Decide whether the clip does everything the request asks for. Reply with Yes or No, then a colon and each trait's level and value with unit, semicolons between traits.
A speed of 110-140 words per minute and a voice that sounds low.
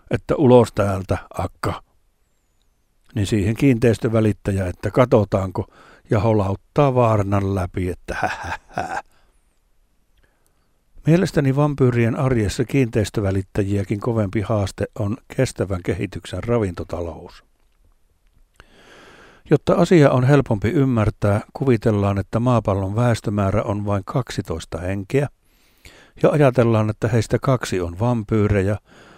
No: slow, 95 wpm; low, 110 Hz